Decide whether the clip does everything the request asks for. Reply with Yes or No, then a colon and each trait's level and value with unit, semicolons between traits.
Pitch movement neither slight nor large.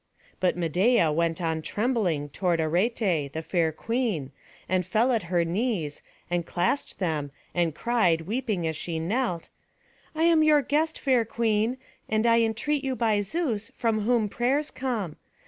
No: wide, 6.4 semitones